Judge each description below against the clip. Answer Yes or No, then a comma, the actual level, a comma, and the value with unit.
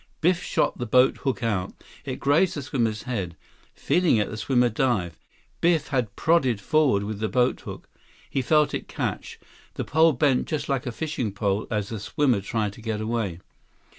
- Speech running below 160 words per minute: No, average, 170 wpm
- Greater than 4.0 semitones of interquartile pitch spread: Yes, wide, 5.4 semitones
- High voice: No, low, 120 Hz